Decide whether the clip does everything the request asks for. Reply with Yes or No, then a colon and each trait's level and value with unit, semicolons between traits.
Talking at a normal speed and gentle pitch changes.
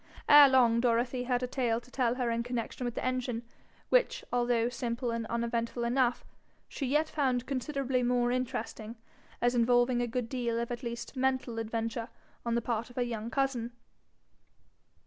Yes: average, 170 wpm; narrow, 1.5 semitones